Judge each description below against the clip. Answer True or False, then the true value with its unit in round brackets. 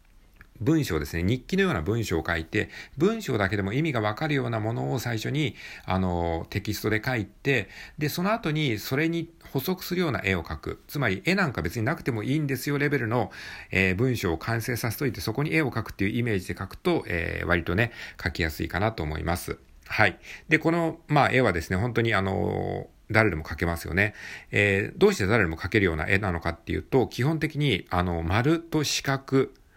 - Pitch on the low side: True (110 Hz)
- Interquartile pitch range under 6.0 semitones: False (7.4 semitones)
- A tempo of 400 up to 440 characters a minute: True (405 characters per minute)